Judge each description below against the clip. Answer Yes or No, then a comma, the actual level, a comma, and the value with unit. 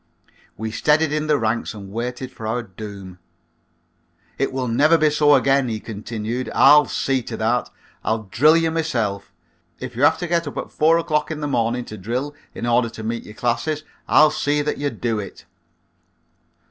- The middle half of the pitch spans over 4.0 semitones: Yes, average, 5.0 semitones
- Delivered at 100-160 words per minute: No, average, 185 wpm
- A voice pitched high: No, low, 125 Hz